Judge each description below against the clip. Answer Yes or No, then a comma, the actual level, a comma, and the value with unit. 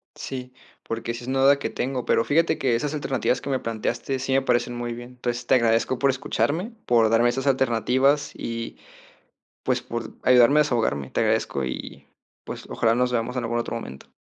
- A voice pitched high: No, low, 125 Hz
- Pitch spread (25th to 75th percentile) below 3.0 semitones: Yes, narrow, 2.4 semitones